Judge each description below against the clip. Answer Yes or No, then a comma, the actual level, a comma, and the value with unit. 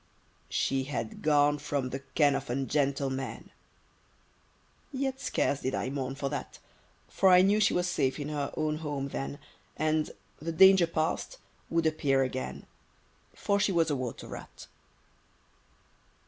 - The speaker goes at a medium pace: Yes, average, 145 wpm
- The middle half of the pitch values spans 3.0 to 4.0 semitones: Yes, average, 3.4 semitones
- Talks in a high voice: No, medium, 145 Hz